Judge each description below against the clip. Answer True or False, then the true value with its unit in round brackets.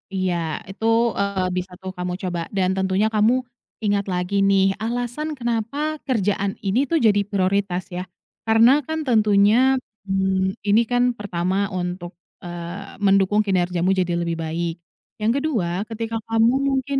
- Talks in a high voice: True (200 Hz)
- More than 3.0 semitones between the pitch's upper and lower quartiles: True (3.7 semitones)